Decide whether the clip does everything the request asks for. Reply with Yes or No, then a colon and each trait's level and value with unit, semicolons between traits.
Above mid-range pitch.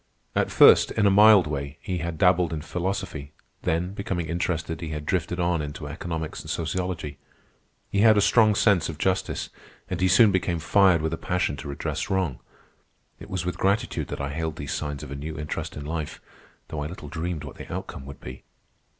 No: very low, 85 Hz